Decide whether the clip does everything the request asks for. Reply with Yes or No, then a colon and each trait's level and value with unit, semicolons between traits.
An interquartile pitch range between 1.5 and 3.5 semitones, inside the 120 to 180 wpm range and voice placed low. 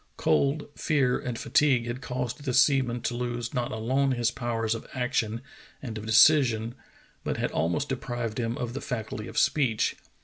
Yes: narrow, 2.5 semitones; average, 175 wpm; low, 120 Hz